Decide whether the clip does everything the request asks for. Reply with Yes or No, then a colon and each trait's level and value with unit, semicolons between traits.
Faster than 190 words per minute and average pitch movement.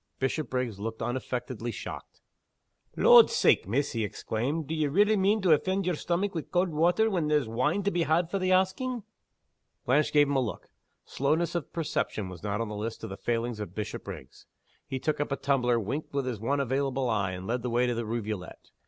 No: fast, 205 wpm; wide, 6.5 semitones